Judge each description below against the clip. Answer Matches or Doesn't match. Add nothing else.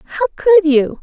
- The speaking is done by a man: Doesn't match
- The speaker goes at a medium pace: Matches